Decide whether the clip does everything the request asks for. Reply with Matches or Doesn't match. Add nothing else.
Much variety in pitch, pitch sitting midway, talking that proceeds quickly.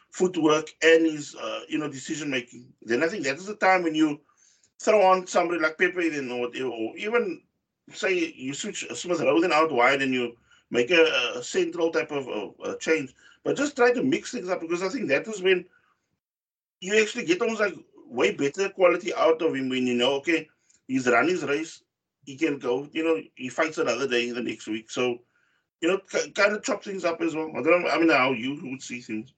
Matches